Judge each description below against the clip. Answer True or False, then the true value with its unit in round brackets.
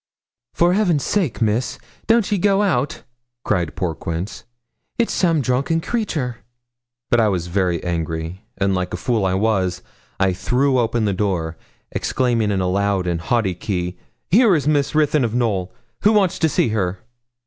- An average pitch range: False (8.5 semitones)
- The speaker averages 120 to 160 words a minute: False (170 wpm)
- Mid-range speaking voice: False (110 Hz)